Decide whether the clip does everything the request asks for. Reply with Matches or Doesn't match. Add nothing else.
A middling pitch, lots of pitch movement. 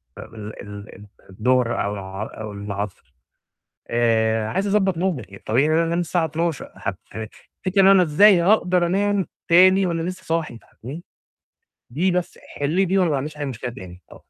Matches